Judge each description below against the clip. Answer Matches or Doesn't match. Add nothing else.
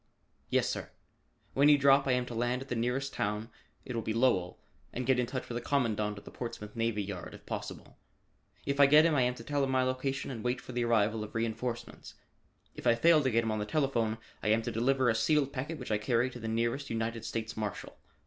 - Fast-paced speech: Matches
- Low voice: Matches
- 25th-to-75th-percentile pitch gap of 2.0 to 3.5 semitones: Matches